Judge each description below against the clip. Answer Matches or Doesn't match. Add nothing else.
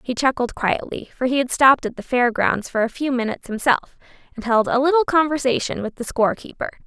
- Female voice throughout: Matches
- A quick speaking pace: Matches